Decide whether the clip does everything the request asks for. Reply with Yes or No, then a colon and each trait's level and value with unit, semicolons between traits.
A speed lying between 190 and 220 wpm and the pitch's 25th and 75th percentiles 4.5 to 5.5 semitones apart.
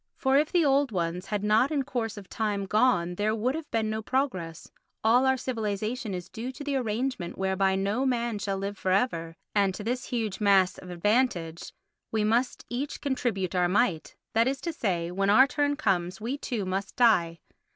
Yes: average, 195 wpm; average, 4.9 semitones